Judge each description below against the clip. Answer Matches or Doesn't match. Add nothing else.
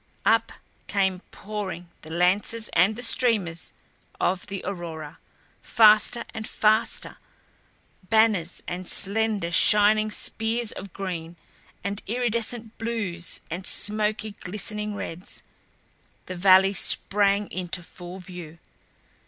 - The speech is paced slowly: Matches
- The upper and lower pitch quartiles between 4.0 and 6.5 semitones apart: Doesn't match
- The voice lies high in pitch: Matches